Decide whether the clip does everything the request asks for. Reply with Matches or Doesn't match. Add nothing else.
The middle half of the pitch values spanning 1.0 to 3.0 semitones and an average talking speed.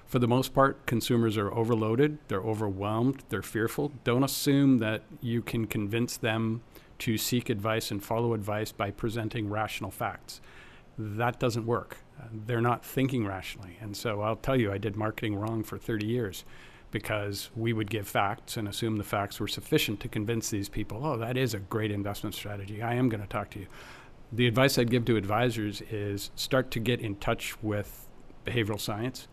Matches